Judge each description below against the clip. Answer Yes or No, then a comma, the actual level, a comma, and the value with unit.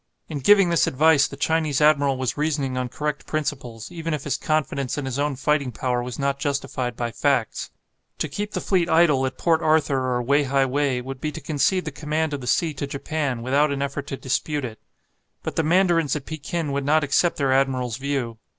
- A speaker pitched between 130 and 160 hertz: Yes, medium, 140 Hz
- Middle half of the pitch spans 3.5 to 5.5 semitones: No, average, 2.7 semitones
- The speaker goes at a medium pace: No, fast, 215 wpm